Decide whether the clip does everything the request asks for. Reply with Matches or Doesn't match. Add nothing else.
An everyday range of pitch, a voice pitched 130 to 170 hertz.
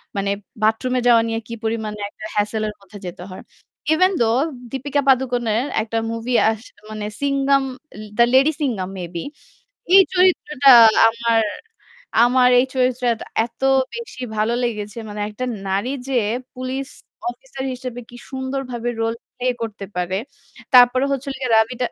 Doesn't match